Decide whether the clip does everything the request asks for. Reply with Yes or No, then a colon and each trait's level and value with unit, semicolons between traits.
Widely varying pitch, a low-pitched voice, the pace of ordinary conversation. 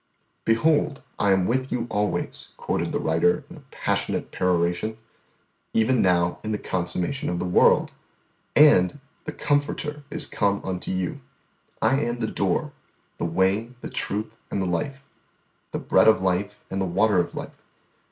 Yes: wide, 6.2 semitones; low, 105 Hz; average, 160 wpm